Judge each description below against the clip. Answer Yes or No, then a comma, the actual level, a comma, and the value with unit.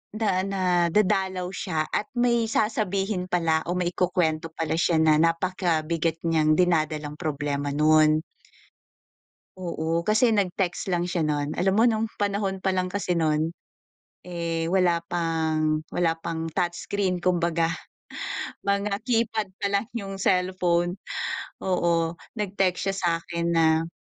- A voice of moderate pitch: Yes, medium, 175 Hz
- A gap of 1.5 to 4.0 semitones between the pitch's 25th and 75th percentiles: Yes, average, 2.9 semitones